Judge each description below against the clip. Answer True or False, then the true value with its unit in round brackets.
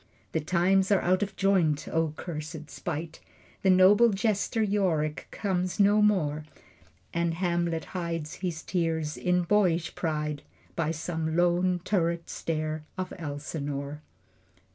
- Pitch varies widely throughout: False (3.0 semitones)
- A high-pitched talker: False (170 Hz)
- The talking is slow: True (125 wpm)